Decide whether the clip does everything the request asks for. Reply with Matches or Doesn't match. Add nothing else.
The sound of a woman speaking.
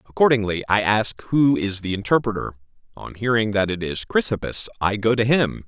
Doesn't match